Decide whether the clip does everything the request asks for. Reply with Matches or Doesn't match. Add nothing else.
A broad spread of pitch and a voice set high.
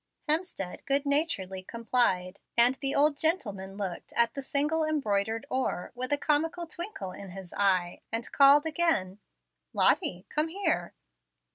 Matches